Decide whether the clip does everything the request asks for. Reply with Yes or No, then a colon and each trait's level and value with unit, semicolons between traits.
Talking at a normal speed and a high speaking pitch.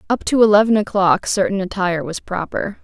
Yes: average, 170 wpm; high, 195 Hz